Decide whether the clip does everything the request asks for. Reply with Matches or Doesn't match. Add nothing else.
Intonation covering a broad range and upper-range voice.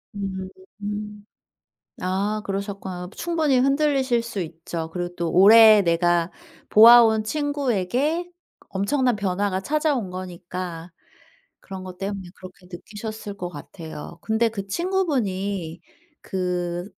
Doesn't match